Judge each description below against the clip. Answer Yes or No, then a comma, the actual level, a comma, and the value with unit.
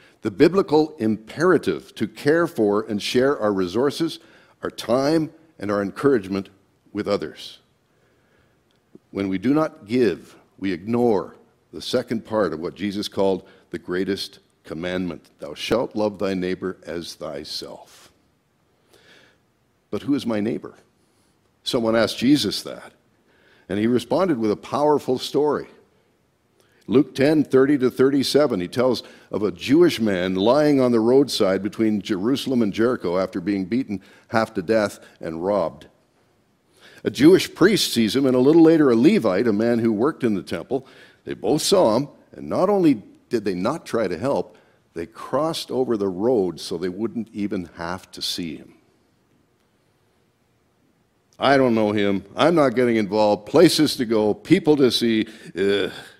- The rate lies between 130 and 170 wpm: Yes, average, 155 wpm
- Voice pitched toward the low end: Yes, low, 110 Hz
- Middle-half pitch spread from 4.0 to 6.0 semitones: Yes, average, 5.0 semitones